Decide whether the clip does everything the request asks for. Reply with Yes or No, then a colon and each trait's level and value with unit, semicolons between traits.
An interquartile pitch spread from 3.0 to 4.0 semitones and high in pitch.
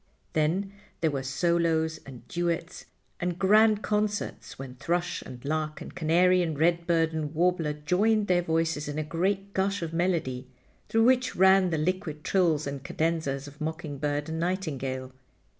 No: average, 3.3 semitones; medium, 165 Hz